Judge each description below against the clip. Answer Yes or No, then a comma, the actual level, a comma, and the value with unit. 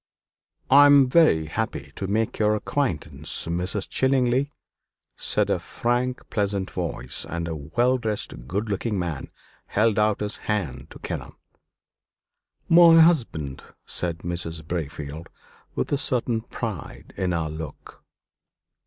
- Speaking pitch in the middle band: No, low, 100 Hz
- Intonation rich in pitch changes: Yes, wide, 7.1 semitones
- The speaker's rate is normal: No, slow, 125 wpm